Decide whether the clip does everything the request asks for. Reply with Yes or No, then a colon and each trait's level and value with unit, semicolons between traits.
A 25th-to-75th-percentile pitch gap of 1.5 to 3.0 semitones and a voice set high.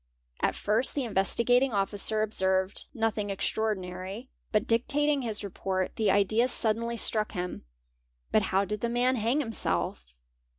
No: average, 3.7 semitones; high, 215 Hz